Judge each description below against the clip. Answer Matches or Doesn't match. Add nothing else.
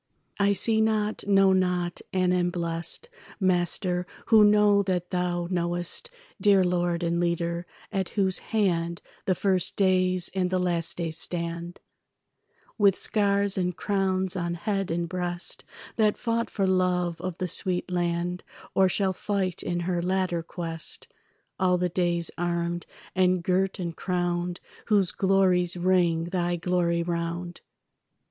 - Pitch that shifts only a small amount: Matches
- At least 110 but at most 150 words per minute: Matches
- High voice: Doesn't match